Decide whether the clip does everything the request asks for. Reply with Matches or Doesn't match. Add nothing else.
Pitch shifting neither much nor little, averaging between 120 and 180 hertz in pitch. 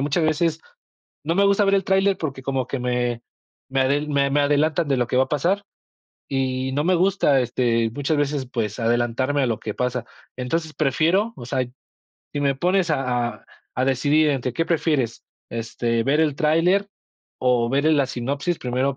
Matches